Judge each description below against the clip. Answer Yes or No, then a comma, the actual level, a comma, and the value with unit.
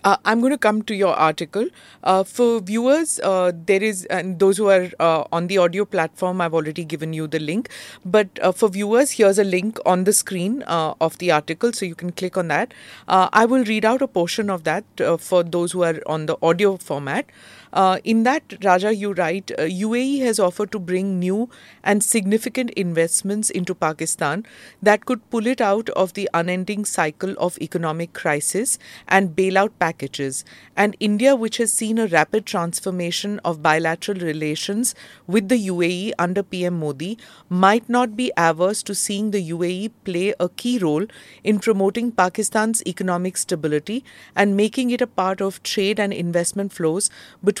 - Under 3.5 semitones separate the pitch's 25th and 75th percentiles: No, average, 3.8 semitones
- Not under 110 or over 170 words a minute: No, average, 185 wpm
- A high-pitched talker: Yes, high, 195 Hz